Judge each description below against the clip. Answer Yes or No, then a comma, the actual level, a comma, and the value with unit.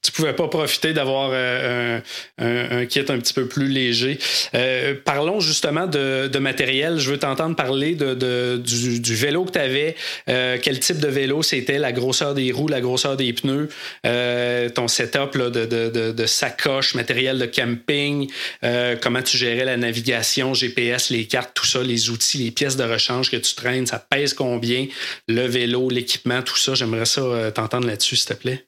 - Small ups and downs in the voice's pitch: Yes, narrow, 2.2 semitones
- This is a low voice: Yes, low, 125 Hz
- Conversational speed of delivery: Yes, average, 195 wpm